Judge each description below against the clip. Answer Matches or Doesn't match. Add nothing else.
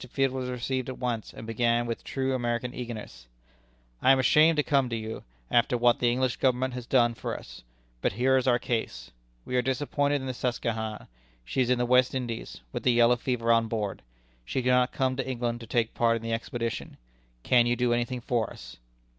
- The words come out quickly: Matches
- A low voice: Matches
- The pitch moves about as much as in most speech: Doesn't match